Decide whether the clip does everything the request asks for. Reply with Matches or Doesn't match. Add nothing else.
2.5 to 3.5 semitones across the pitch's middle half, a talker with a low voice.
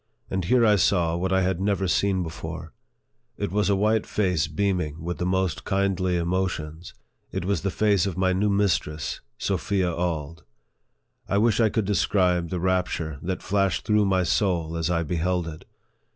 Matches